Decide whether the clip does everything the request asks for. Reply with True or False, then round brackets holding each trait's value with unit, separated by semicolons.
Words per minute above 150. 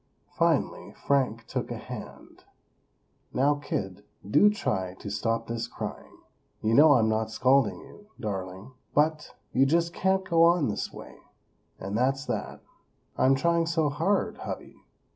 False (145 wpm)